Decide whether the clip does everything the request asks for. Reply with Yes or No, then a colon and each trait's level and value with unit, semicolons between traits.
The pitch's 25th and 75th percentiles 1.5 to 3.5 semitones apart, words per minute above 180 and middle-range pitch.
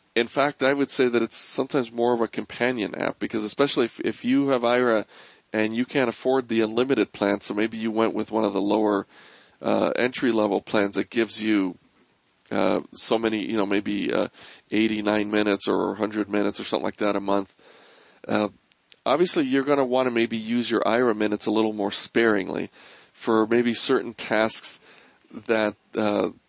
No: narrow, 2.6 semitones; average, 190 wpm; low, 110 Hz